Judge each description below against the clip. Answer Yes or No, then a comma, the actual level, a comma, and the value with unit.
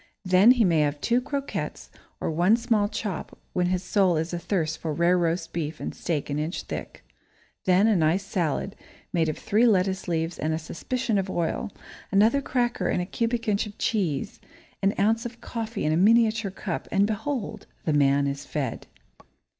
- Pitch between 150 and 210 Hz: Yes, medium, 185 Hz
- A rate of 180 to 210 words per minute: Yes, average, 185 wpm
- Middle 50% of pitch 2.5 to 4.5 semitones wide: No, average, 5.2 semitones